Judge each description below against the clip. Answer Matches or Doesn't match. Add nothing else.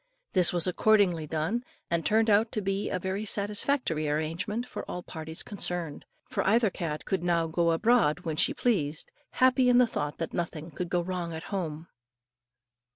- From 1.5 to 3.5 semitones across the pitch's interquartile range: Doesn't match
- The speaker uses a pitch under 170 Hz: Doesn't match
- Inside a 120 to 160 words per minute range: Doesn't match